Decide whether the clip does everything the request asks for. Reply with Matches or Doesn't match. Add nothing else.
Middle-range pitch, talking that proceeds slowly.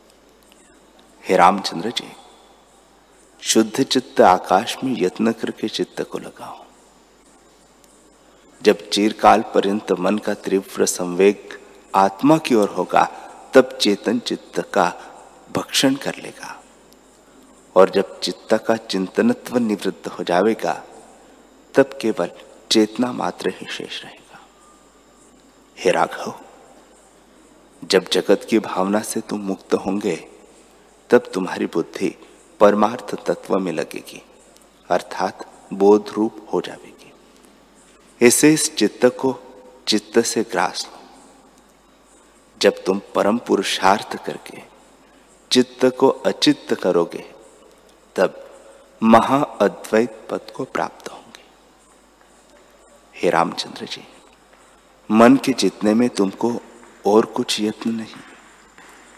Doesn't match